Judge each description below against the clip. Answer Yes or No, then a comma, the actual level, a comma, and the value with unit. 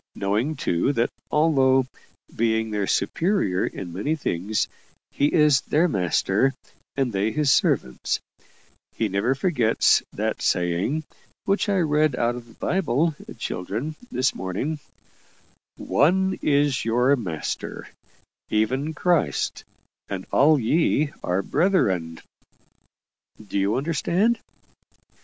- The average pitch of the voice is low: Yes, low, 130 Hz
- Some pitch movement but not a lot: No, wide, 7.3 semitones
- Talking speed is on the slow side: Yes, slow, 110 wpm